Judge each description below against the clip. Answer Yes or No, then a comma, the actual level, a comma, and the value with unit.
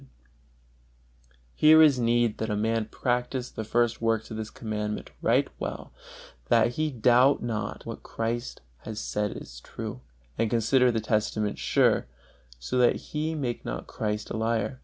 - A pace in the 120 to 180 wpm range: Yes, average, 160 wpm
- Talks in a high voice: No, low, 115 Hz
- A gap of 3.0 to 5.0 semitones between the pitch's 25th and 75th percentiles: No, narrow, 2.5 semitones